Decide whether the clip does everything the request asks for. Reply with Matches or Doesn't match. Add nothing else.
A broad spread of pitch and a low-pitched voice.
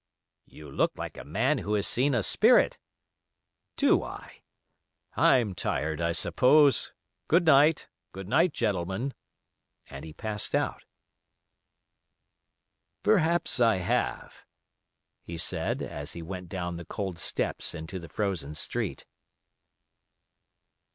Matches